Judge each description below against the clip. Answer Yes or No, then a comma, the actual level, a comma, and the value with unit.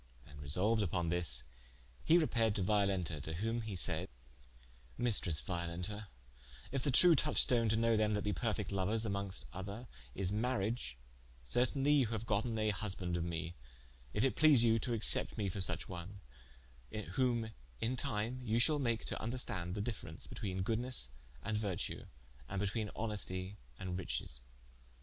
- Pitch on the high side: No, low, 105 Hz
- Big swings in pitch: No, average, 4.0 semitones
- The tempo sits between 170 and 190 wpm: No, average, 160 wpm